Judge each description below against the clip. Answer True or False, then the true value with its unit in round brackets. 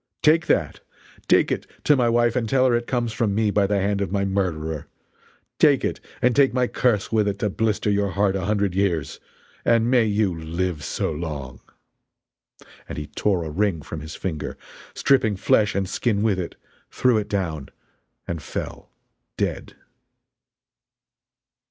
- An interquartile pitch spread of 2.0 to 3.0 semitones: False (4.5 semitones)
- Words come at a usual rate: True (170 wpm)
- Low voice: True (100 Hz)